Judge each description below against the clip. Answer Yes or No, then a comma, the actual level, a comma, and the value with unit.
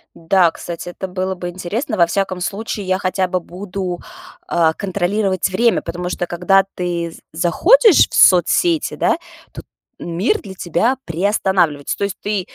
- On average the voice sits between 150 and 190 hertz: Yes, medium, 185 Hz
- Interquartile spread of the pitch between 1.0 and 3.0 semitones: Yes, narrow, 2.4 semitones